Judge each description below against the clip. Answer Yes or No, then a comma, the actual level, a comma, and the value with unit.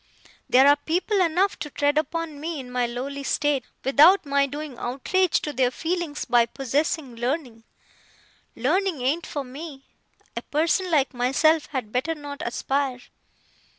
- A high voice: Yes, very high, 285 Hz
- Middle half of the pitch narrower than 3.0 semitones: No, average, 3.8 semitones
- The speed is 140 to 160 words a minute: Yes, average, 150 wpm